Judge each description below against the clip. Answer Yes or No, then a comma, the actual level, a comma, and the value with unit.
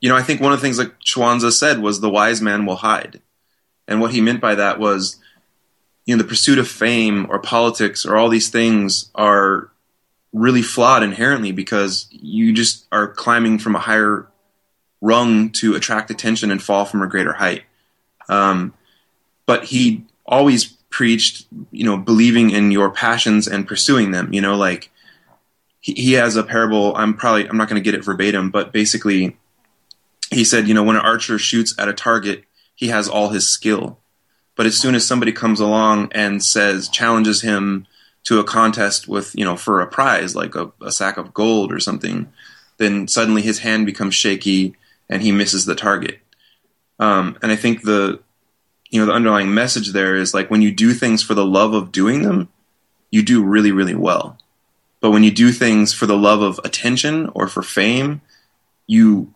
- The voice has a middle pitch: No, low, 110 Hz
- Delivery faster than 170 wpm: Yes, average, 190 wpm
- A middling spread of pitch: No, narrow, 2.3 semitones